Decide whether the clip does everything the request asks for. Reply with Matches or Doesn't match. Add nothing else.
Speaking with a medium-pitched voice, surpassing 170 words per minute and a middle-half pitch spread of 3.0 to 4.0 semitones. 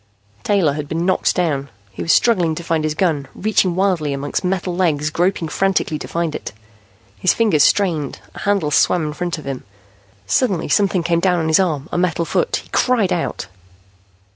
Matches